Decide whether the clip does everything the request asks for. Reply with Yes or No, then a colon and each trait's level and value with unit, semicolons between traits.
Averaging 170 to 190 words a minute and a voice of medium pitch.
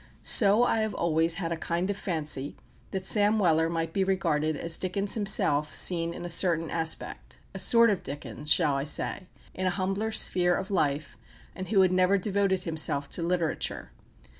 Yes: average, 185 wpm; medium, 175 Hz